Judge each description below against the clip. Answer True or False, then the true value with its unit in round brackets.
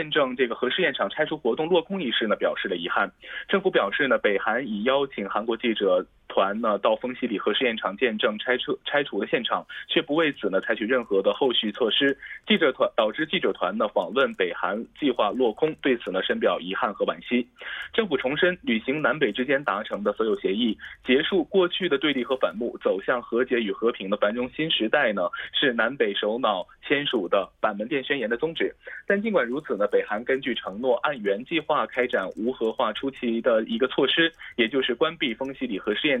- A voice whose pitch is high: False (135 Hz)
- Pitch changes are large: True (7.3 semitones)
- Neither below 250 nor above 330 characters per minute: True (320 characters per minute)